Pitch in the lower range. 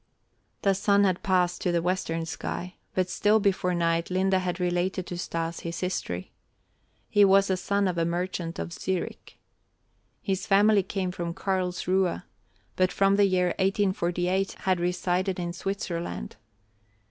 No: medium, 185 Hz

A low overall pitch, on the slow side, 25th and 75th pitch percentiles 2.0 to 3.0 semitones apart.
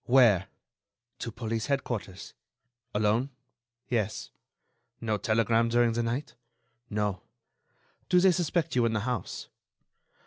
Yes: low, 115 Hz; slow, 110 wpm; average, 2.7 semitones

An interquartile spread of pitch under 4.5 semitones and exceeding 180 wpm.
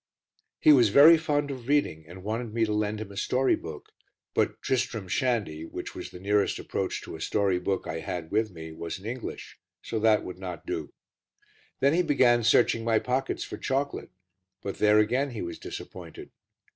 No: wide, 5.4 semitones; average, 190 wpm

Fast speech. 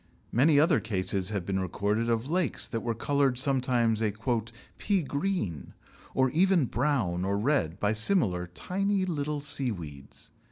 No: average, 145 wpm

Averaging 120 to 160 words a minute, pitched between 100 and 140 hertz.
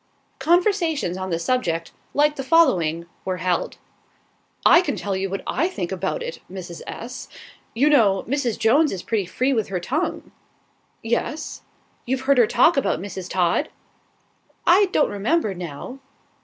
No: average, 155 wpm; high, 230 Hz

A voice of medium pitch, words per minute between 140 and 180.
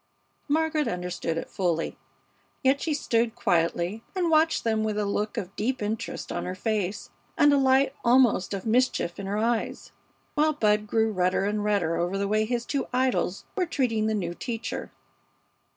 No: high, 220 Hz; average, 175 wpm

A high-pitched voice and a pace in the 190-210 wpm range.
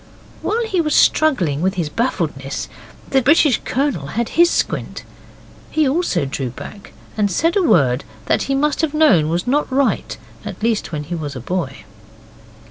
No: high, 220 Hz; average, 170 wpm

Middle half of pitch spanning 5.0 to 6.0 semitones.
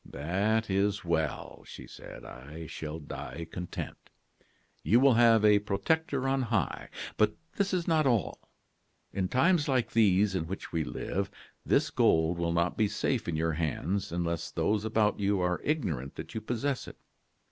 Yes: wide, 5.6 semitones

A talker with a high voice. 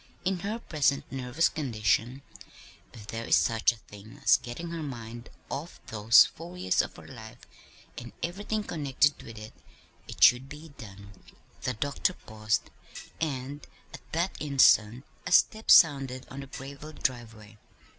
No: low, 130 Hz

